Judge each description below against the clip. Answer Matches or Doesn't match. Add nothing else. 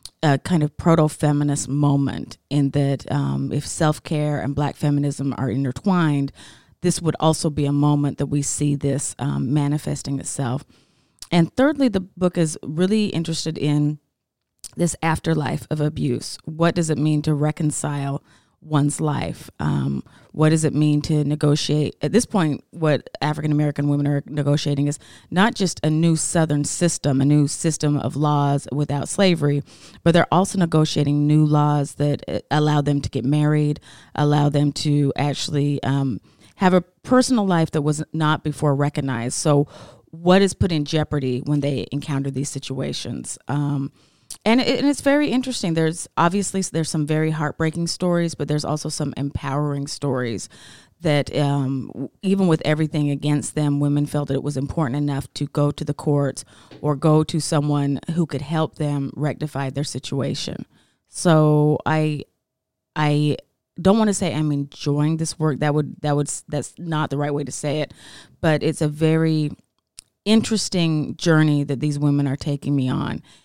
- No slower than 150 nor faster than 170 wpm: Matches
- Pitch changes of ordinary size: Doesn't match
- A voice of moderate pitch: Matches